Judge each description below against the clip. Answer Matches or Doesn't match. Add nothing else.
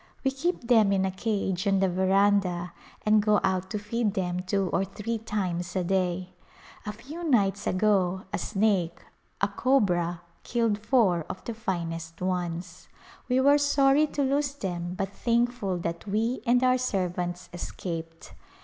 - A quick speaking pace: Doesn't match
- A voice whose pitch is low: Doesn't match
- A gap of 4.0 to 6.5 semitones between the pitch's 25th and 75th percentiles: Matches